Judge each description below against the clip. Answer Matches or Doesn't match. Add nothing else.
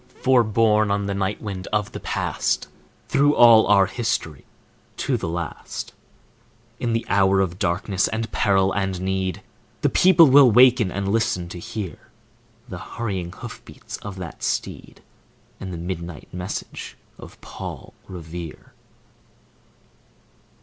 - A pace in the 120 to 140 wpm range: Matches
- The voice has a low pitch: Matches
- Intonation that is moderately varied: Matches